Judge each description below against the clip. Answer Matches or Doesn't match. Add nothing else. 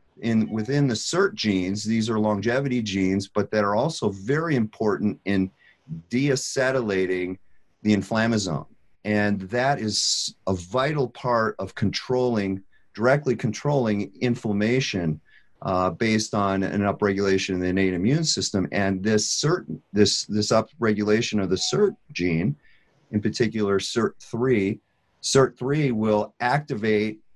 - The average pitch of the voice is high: Doesn't match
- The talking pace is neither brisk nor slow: Doesn't match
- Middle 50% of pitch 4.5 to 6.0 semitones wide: Doesn't match